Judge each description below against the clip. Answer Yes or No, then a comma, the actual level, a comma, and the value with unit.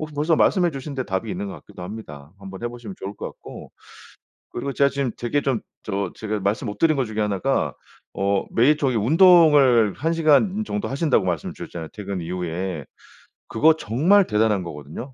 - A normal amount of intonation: No, wide, 7.3 semitones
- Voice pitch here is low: Yes, low, 120 Hz